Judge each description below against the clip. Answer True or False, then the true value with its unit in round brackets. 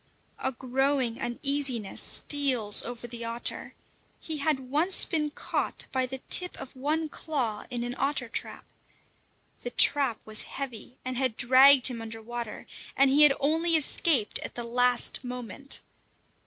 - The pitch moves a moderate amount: True (3.1 semitones)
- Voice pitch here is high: True (260 Hz)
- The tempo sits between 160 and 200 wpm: False (150 wpm)